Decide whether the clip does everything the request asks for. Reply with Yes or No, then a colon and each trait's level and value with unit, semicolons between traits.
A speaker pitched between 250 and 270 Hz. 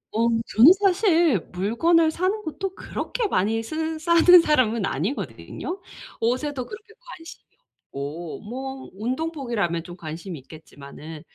Yes: very high, 255 Hz